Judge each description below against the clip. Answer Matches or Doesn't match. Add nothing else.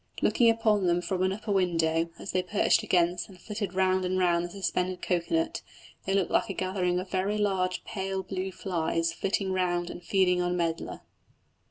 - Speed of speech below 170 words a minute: Doesn't match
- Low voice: Doesn't match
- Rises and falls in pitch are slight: Matches